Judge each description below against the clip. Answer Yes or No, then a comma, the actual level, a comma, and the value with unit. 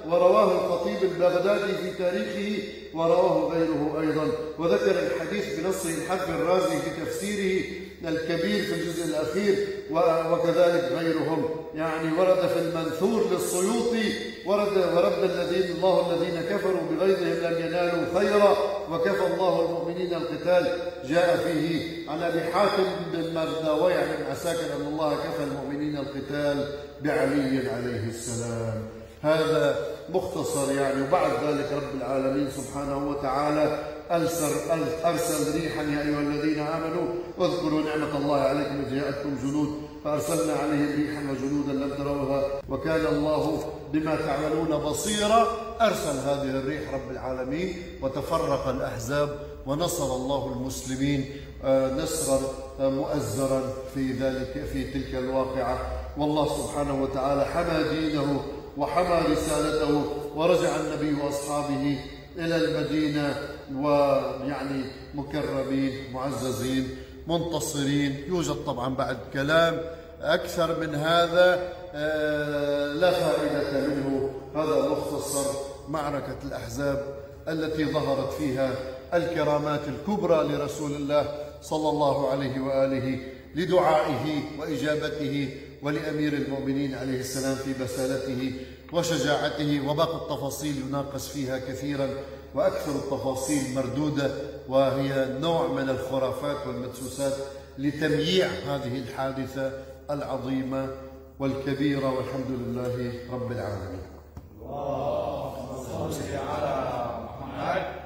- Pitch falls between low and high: Yes, medium, 145 Hz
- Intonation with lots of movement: No, average, 3.4 semitones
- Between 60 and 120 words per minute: Yes, average, 100 wpm